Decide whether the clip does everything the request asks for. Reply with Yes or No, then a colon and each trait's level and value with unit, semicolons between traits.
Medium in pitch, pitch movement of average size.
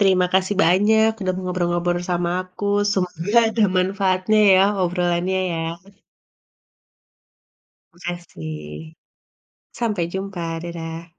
No: medium, 180 Hz; narrow, 1.9 semitones